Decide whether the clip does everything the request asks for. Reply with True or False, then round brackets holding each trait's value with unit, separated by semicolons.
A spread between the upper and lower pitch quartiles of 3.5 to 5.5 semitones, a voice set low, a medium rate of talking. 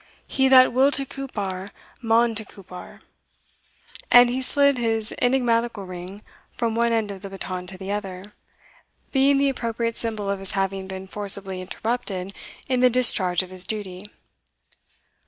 False (4.2 semitones; 215 Hz; 155 wpm)